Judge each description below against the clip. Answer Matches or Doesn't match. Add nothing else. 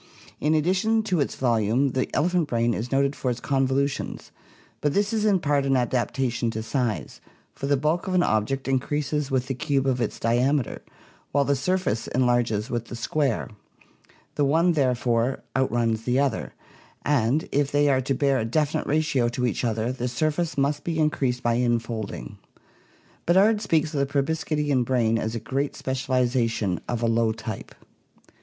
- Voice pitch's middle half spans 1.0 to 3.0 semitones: Doesn't match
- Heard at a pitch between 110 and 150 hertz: Matches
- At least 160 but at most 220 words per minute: Matches